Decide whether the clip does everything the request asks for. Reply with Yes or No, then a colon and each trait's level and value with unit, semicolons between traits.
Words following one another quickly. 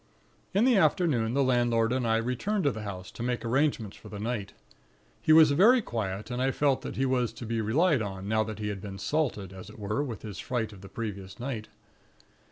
Yes: fast, 220 wpm